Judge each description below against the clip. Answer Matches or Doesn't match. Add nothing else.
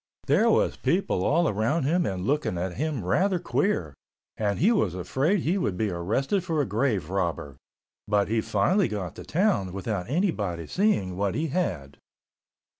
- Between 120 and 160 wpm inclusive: Doesn't match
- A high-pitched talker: Doesn't match